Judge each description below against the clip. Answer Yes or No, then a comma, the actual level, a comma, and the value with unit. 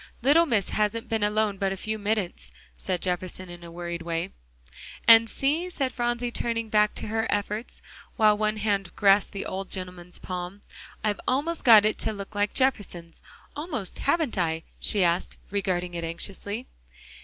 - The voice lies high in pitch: Yes, high, 205 Hz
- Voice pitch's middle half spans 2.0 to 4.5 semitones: Yes, average, 3.8 semitones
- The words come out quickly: No, average, 165 wpm